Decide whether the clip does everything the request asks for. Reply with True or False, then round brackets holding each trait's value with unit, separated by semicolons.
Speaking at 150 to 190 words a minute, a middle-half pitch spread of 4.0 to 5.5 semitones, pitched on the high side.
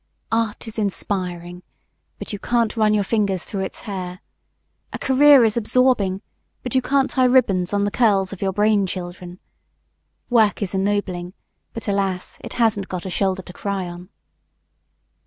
False (160 wpm; 3.4 semitones; 200 Hz)